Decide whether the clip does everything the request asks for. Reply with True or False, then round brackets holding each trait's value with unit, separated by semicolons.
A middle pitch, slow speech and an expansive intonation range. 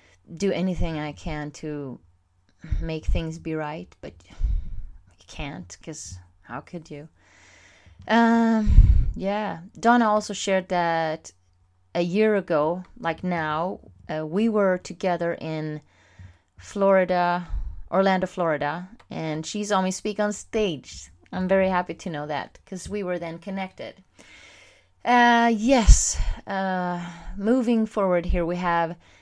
False (175 Hz; 125 wpm; 4.7 semitones)